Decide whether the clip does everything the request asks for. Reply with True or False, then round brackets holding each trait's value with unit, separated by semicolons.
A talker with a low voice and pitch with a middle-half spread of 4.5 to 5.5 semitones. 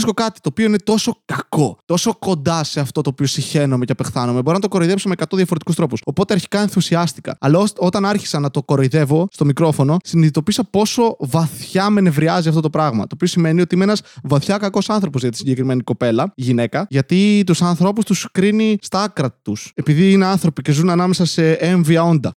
False (170 Hz; 5.1 semitones)